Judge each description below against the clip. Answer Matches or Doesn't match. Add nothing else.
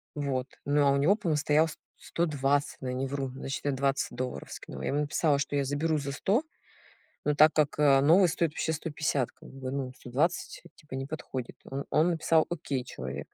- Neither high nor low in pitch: Matches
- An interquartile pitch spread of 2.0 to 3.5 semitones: Matches